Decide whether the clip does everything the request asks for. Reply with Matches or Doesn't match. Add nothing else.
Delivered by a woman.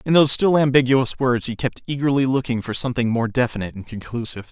Doesn't match